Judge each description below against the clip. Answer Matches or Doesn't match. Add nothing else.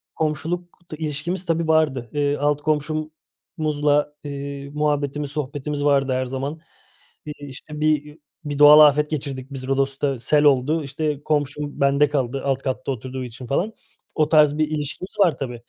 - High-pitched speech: Doesn't match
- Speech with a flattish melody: Matches